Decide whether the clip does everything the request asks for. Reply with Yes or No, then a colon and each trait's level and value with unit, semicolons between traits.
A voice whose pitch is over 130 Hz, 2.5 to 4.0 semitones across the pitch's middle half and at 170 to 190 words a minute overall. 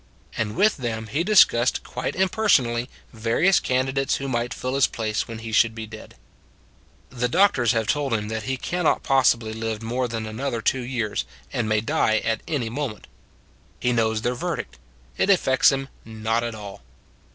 No: low, 120 Hz; average, 3.2 semitones; average, 175 wpm